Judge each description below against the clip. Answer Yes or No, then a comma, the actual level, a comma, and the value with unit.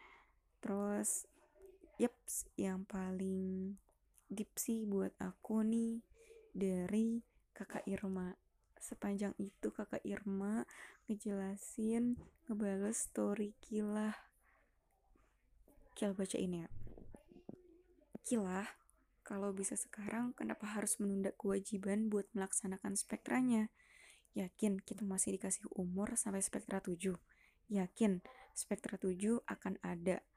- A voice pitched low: No, high, 205 Hz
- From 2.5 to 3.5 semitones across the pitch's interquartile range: Yes, average, 2.9 semitones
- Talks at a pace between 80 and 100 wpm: Yes, average, 95 wpm